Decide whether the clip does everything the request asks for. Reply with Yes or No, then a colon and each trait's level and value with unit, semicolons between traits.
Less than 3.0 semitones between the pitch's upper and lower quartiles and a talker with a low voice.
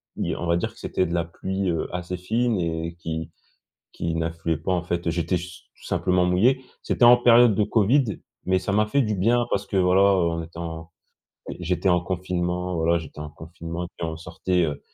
Yes: narrow, 2.5 semitones; very low, 90 Hz